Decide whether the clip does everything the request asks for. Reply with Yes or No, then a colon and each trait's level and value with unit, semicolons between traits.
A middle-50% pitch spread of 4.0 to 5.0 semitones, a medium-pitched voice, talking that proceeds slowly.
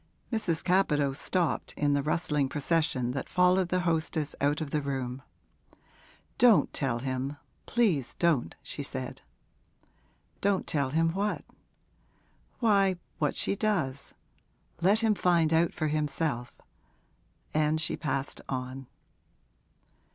Yes: average, 4.7 semitones; medium, 155 Hz; slow, 120 wpm